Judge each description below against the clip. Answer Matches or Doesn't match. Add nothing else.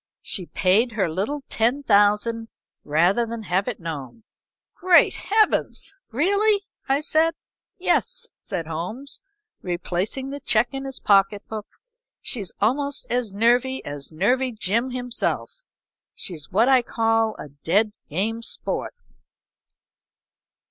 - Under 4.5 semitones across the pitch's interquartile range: Doesn't match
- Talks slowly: Matches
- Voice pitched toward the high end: Matches